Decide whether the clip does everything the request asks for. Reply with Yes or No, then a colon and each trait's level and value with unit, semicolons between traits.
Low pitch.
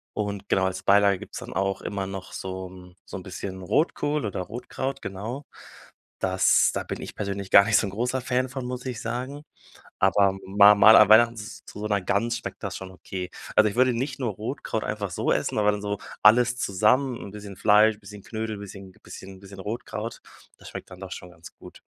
Yes: low, 105 Hz